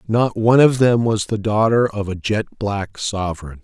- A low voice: Yes, low, 110 Hz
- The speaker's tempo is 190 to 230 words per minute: Yes, average, 200 wpm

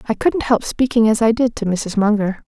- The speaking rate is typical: No, fast, 245 wpm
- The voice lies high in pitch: Yes, high, 220 Hz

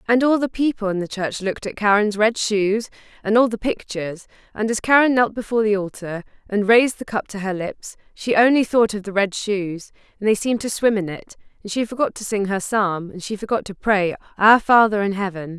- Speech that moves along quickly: Yes, fast, 230 wpm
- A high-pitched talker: Yes, high, 210 Hz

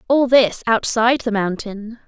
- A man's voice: No, female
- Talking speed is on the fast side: No, average, 145 wpm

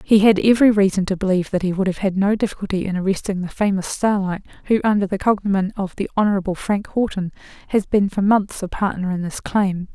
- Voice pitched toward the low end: No, high, 195 Hz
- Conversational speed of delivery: No, fast, 215 wpm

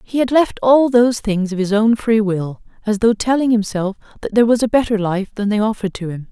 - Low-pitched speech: No, high, 215 Hz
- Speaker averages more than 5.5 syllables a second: Yes, 5.9 syllables/s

